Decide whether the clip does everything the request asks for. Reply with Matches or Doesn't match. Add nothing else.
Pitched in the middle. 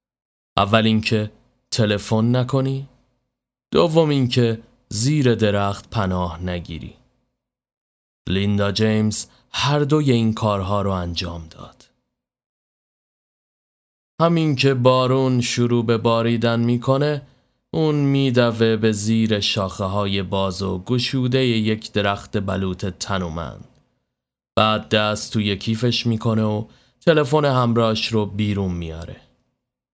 Doesn't match